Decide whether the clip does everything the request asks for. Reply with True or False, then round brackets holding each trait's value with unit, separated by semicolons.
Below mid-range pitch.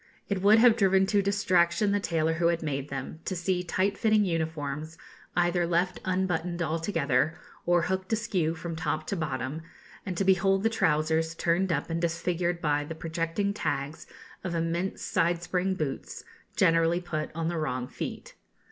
False (170 Hz)